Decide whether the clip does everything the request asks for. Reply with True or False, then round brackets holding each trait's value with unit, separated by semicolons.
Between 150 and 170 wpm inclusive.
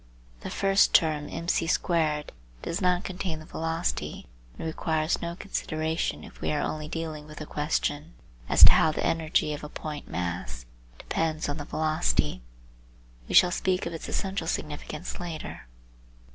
True (155 wpm)